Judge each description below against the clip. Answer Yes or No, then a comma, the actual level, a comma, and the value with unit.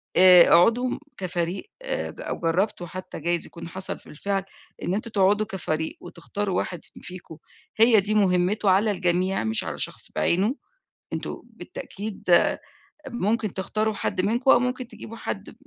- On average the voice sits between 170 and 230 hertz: Yes, high, 190 Hz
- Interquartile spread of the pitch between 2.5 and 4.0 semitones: Yes, average, 3.5 semitones